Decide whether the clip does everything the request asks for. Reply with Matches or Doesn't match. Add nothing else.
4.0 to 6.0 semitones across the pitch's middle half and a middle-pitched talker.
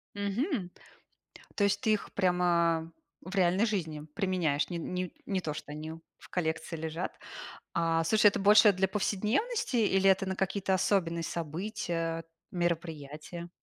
Doesn't match